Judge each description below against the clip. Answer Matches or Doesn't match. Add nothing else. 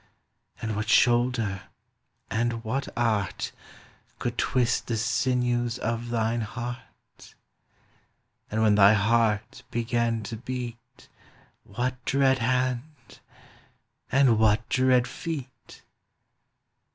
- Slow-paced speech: Matches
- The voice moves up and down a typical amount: Doesn't match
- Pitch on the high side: Doesn't match